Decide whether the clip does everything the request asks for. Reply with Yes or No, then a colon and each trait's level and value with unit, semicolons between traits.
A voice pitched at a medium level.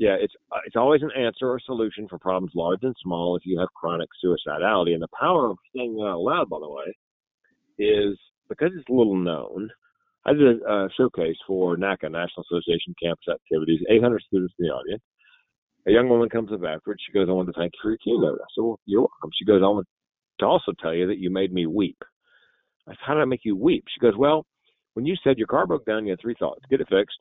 No: low, 105 Hz